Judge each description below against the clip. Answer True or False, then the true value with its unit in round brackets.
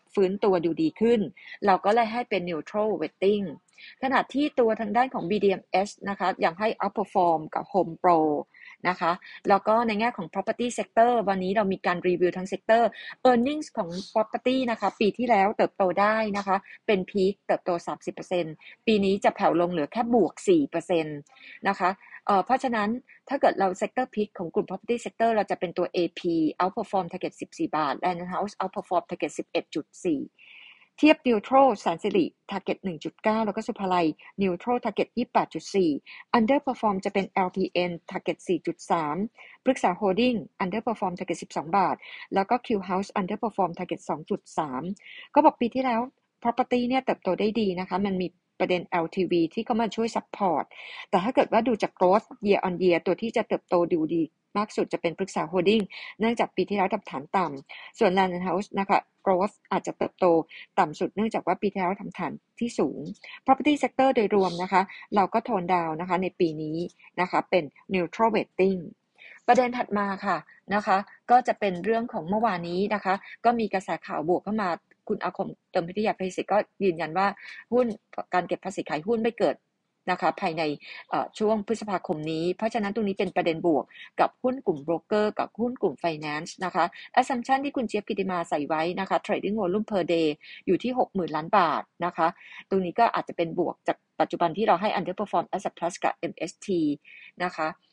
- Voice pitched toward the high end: True (195 Hz)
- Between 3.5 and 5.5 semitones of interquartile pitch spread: True (4.2 semitones)